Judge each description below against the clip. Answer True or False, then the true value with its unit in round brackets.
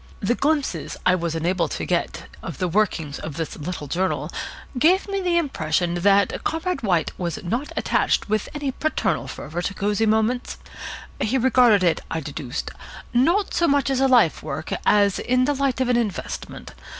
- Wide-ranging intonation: True (7.4 semitones)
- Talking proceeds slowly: False (175 wpm)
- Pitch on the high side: True (215 Hz)